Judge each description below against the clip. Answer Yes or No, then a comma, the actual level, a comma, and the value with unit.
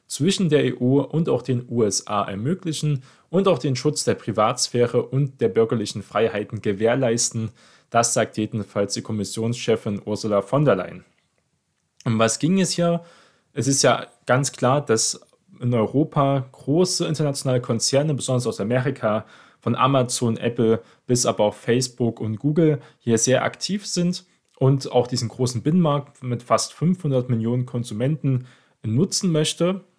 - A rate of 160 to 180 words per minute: No, average, 145 wpm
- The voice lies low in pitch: Yes, low, 125 Hz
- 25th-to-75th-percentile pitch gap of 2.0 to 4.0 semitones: No, average, 4.5 semitones